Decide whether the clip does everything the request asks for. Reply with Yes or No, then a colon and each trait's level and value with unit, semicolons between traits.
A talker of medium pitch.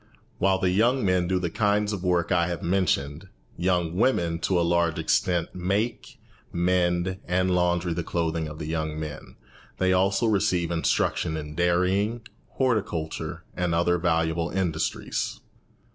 No: very low, 90 Hz